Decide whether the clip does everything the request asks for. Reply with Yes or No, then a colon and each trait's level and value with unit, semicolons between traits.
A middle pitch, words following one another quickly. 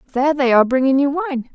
No: very high, 275 Hz; fast, 235 wpm